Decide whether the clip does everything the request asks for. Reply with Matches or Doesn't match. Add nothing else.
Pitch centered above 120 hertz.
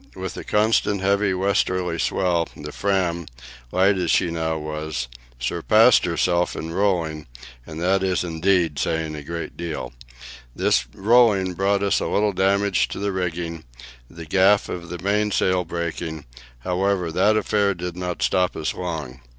Doesn't match